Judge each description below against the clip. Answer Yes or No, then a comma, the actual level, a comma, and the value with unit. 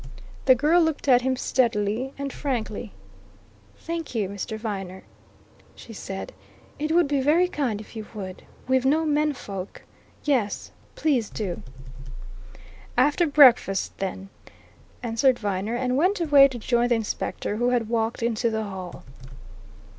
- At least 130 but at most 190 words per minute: Yes, average, 140 wpm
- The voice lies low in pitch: No, high, 245 Hz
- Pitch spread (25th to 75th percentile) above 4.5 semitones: Yes, average, 5.1 semitones